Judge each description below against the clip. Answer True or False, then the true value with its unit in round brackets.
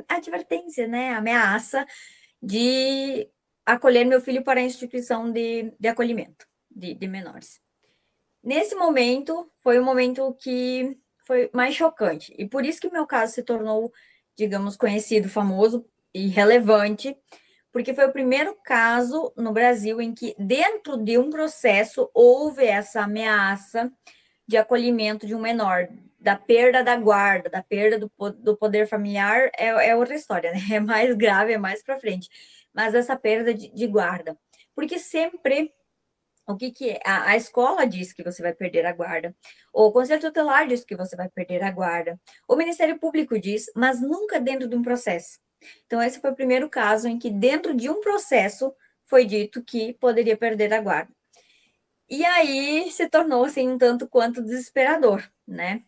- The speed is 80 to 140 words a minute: False (165 wpm)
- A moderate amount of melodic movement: True (3.9 semitones)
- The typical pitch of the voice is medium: False (240 Hz)